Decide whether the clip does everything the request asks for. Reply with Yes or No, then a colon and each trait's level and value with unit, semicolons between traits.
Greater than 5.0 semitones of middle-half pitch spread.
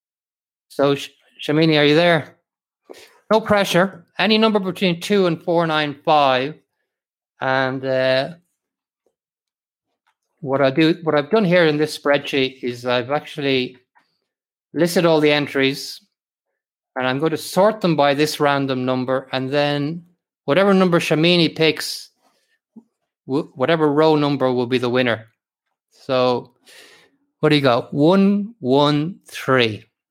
No: average, 4.6 semitones